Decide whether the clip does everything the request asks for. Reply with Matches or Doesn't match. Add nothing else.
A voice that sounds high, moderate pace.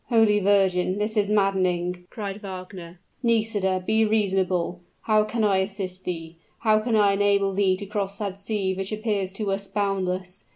Matches